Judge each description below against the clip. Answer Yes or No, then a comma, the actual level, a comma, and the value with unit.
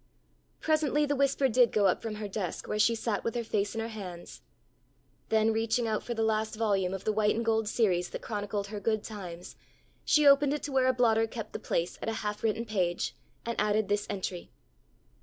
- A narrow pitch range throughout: Yes, narrow, 2.2 semitones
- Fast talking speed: Yes, fast, 215 wpm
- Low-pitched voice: No, high, 220 Hz